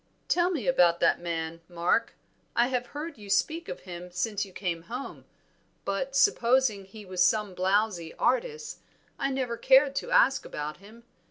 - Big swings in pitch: Yes, wide, 6.6 semitones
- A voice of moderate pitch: No, high, 215 Hz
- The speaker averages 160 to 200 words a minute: Yes, average, 165 wpm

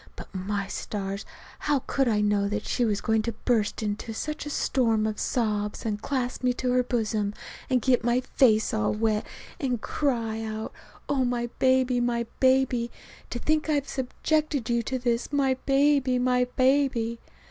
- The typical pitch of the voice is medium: No, high, 240 Hz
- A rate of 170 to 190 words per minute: Yes, average, 175 wpm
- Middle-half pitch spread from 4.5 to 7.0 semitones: No, average, 3.2 semitones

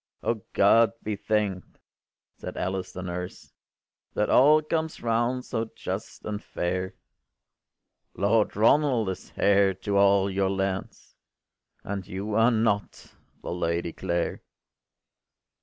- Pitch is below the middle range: Yes, low, 100 Hz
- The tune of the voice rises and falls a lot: No, average, 3.1 semitones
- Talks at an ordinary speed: No, slow, 125 wpm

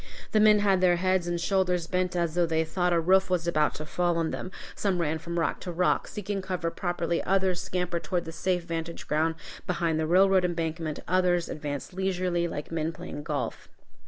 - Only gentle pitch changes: Yes, narrow, 1.9 semitones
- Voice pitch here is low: No, medium, 175 Hz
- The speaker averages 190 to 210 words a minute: Yes, average, 200 wpm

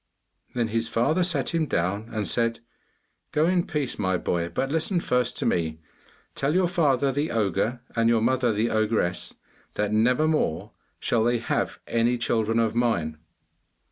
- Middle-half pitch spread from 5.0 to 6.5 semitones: No, average, 4.2 semitones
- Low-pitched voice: Yes, low, 115 Hz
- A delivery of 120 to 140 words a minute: No, average, 165 wpm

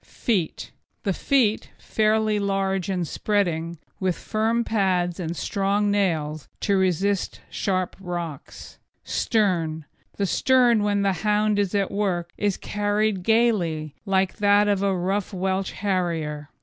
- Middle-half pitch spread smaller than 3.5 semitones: Yes, average, 2.8 semitones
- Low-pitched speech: No, high, 195 Hz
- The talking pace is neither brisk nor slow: No, slow, 130 wpm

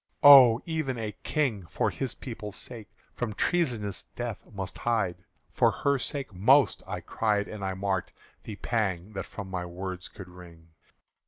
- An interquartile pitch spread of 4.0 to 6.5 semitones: Yes, average, 4.5 semitones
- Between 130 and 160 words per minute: Yes, average, 155 wpm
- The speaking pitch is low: Yes, low, 105 Hz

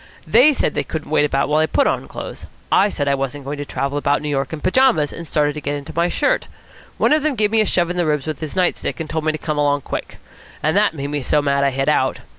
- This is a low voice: No, medium, 150 Hz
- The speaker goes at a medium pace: No, fast, 290 wpm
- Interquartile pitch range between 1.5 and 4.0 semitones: Yes, average, 3.5 semitones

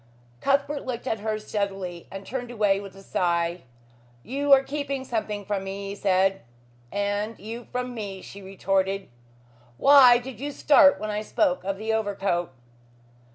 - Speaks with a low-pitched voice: No, high, 210 Hz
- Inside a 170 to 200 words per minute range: No, average, 155 wpm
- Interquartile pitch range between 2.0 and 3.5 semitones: No, average, 4.3 semitones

